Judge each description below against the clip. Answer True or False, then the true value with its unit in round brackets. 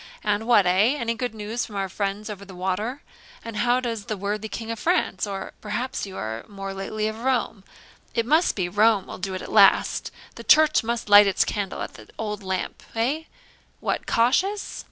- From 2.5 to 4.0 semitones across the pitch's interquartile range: True (3.2 semitones)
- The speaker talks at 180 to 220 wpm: True (200 wpm)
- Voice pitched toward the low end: False (215 Hz)